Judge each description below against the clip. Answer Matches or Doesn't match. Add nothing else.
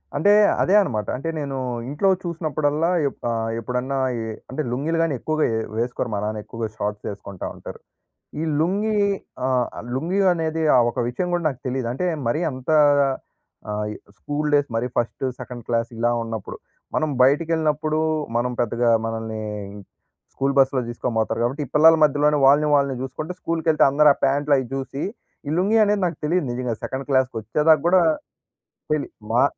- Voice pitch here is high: Doesn't match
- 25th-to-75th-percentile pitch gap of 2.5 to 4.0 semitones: Doesn't match